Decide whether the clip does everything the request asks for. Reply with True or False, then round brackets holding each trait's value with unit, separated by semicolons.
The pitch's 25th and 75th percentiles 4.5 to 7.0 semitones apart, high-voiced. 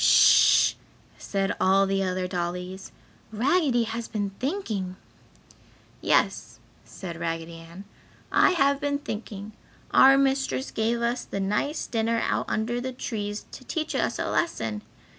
True (5.5 semitones; 220 Hz)